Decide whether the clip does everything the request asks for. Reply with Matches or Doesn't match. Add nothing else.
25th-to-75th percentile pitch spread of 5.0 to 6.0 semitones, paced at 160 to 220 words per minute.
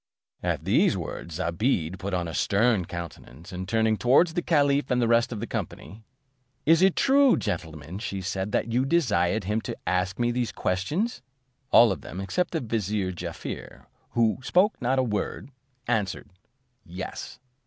Matches